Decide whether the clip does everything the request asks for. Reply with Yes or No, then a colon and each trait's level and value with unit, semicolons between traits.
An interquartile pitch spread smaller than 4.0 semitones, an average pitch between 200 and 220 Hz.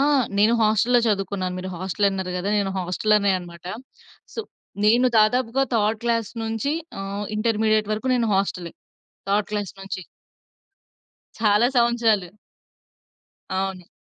Yes: average, 2.8 semitones; high, 210 Hz